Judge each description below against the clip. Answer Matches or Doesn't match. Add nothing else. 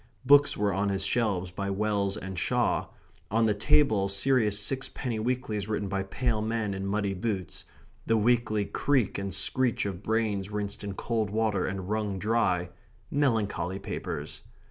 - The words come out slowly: Doesn't match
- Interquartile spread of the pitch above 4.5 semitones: Doesn't match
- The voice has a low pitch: Matches